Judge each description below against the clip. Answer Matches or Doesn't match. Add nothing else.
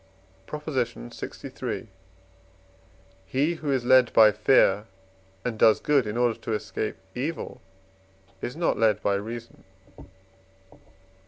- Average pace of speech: Doesn't match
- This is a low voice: Matches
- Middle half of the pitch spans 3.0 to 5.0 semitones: Matches